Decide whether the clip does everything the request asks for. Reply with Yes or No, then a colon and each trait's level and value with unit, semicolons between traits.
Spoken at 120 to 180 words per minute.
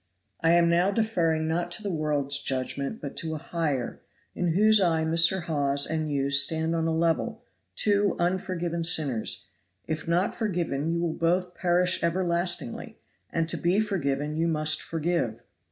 Yes: average, 160 wpm